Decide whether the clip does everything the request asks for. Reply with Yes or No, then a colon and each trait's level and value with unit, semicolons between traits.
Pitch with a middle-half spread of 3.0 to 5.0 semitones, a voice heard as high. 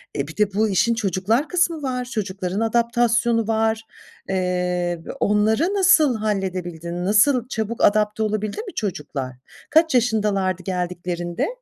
Yes: average, 4.4 semitones; high, 210 Hz